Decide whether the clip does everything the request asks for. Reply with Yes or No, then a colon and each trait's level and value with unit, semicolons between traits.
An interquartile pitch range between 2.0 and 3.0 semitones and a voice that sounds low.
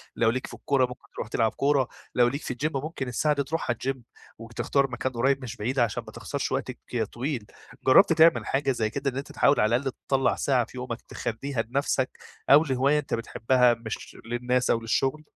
Yes: average, 2.7 semitones; low, 130 Hz